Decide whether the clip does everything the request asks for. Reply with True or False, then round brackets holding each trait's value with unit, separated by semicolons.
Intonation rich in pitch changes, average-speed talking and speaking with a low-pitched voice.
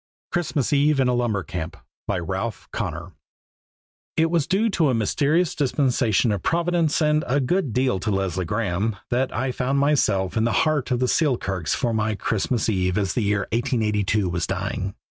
True (6.3 semitones; 180 wpm; 115 Hz)